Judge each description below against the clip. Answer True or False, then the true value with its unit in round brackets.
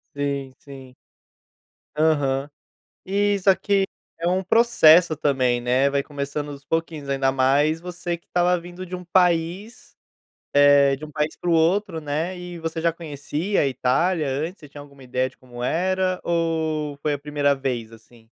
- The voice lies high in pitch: False (155 Hz)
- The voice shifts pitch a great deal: False (4.0 semitones)